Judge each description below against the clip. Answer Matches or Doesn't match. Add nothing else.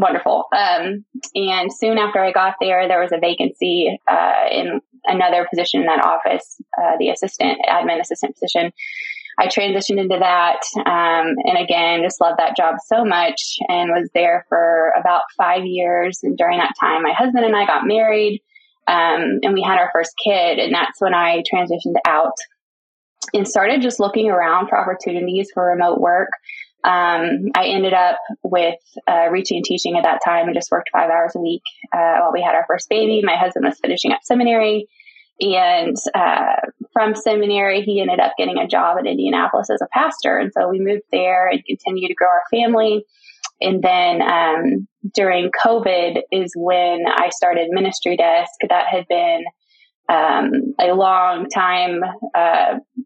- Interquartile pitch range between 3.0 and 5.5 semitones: Matches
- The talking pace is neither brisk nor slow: Matches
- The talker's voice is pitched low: Doesn't match